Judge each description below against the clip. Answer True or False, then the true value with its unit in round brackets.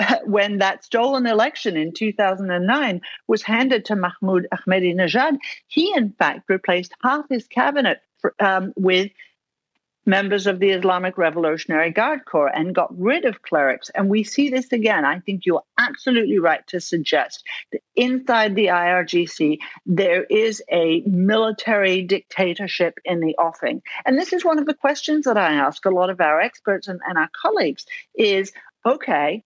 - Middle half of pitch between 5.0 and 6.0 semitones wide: True (5.4 semitones)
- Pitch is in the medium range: False (200 Hz)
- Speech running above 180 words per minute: False (160 wpm)